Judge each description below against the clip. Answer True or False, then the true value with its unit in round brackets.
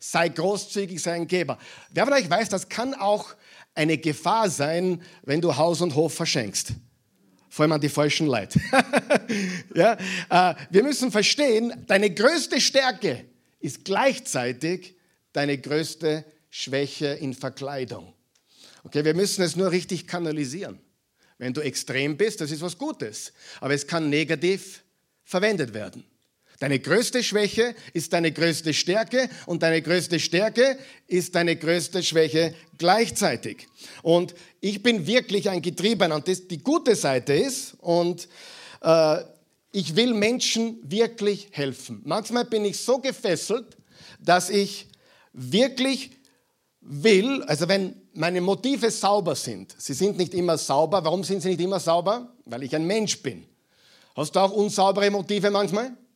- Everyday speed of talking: True (145 wpm)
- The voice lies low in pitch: False (180 Hz)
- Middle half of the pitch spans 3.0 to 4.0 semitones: False (5.2 semitones)